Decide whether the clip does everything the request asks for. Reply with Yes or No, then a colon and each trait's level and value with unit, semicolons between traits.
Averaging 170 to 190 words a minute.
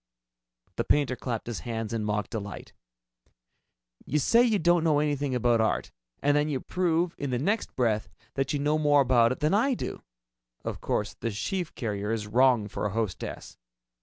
Yes: average, 185 wpm